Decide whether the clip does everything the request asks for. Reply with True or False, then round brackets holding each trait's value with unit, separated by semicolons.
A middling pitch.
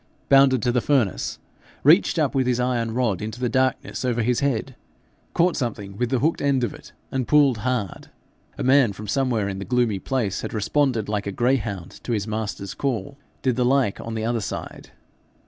False (120 Hz)